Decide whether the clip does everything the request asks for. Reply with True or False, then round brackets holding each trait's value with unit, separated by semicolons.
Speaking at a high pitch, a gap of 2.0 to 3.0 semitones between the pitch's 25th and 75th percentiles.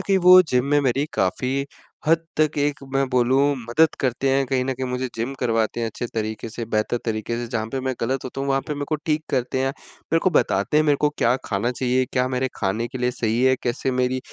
False (130 Hz; 2.6 semitones)